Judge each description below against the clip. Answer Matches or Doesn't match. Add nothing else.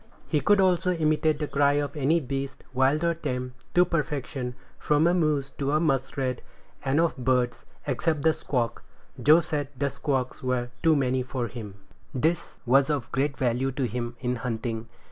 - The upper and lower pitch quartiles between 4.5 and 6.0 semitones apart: Doesn't match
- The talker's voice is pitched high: Doesn't match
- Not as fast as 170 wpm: Doesn't match